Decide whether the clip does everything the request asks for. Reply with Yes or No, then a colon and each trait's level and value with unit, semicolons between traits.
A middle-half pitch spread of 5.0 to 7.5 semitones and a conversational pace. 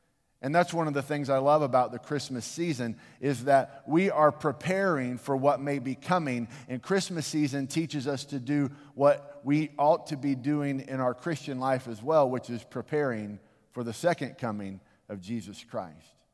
No: average, 3.2 semitones; average, 185 wpm